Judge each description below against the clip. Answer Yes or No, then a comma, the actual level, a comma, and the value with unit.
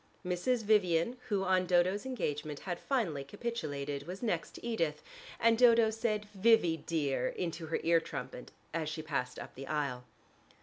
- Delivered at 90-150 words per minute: No, average, 160 wpm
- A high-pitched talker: No, medium, 175 Hz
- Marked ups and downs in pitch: Yes, wide, 6.4 semitones